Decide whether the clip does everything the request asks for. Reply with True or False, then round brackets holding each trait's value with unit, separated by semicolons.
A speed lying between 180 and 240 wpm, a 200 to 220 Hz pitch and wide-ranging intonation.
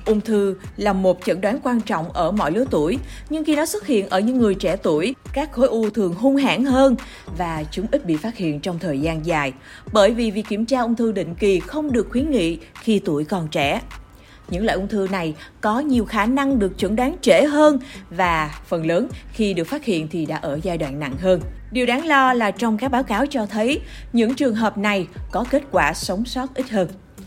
True (230 wpm; 210 Hz; 6.0 semitones)